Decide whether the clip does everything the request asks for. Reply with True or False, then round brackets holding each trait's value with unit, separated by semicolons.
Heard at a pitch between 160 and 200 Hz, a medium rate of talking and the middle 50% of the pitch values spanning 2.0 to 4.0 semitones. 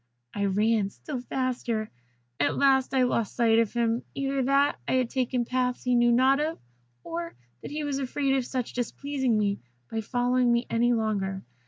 False (245 Hz; 175 wpm; 2.9 semitones)